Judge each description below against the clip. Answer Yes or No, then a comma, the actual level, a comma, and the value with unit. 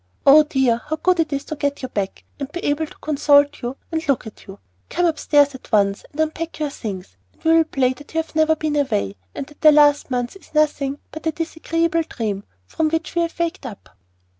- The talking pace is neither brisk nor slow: No, fast, 230 wpm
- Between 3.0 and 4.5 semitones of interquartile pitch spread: Yes, average, 3.7 semitones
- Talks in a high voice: Yes, very high, 295 Hz